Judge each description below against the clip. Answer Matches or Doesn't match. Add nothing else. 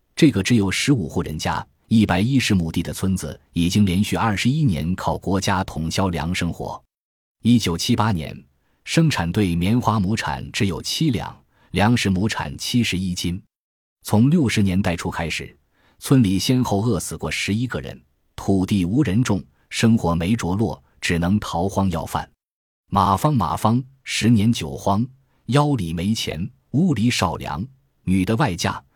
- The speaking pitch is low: Matches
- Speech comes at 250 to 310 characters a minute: Doesn't match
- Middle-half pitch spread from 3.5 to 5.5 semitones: Matches